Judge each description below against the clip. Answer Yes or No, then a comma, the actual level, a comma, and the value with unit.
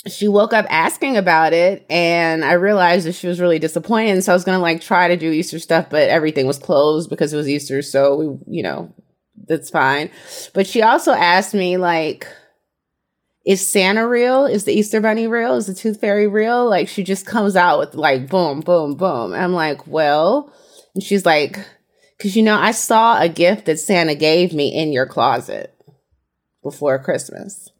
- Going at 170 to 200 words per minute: Yes, average, 195 wpm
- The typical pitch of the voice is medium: Yes, medium, 180 Hz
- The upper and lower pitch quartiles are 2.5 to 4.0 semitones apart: No, average, 4.7 semitones